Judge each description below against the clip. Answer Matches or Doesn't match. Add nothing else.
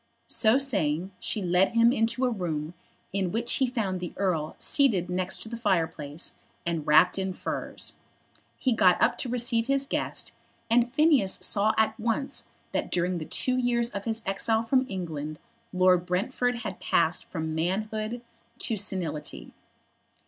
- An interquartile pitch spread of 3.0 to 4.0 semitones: Doesn't match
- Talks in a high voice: Matches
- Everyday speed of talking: Matches